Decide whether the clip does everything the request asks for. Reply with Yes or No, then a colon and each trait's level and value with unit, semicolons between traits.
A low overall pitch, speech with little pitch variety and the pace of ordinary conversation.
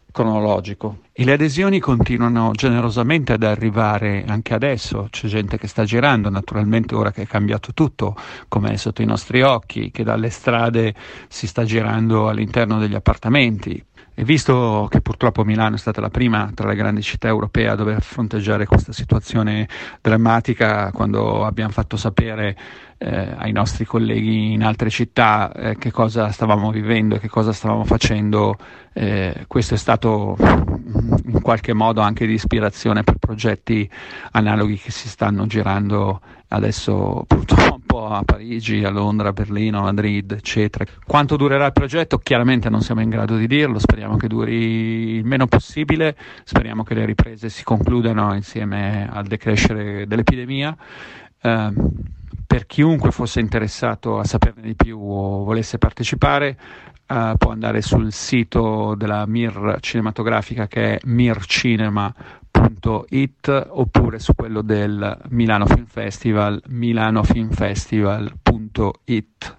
Yes: low, 110 Hz; narrow, 1.8 semitones; average, 145 wpm